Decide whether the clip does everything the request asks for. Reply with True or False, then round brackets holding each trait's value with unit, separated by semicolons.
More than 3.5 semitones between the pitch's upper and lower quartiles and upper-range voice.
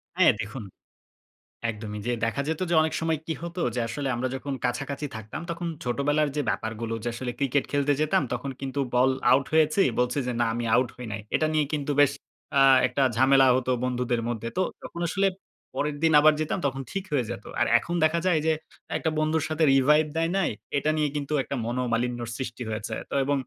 False (4.0 semitones; 140 Hz)